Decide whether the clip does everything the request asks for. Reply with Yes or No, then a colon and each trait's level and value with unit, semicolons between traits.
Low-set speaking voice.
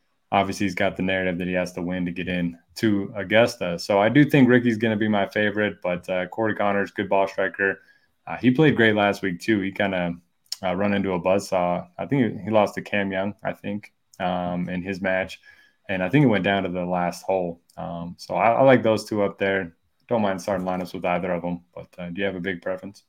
Yes: very low, 95 Hz